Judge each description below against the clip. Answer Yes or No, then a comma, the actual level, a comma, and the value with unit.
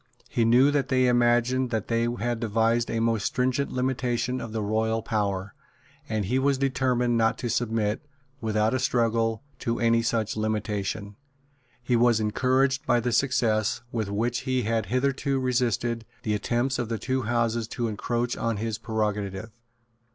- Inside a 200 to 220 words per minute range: No, average, 160 wpm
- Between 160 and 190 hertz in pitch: No, low, 115 Hz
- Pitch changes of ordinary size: No, narrow, 2.3 semitones